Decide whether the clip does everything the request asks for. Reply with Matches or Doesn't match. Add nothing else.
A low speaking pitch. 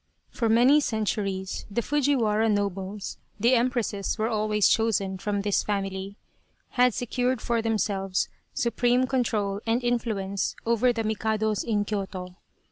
Doesn't match